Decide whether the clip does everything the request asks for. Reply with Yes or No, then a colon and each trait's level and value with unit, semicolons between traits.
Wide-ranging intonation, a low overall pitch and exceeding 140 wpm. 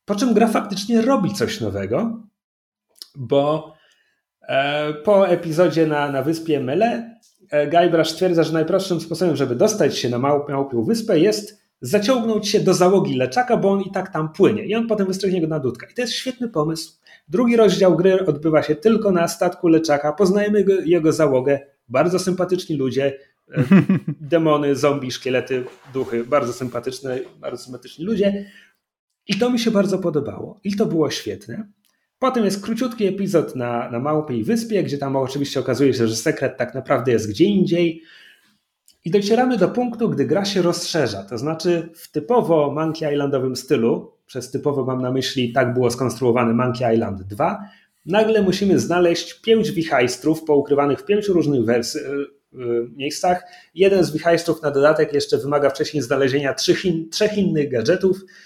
No: wide, 6.1 semitones; medium, 160 Hz; fast, 160 wpm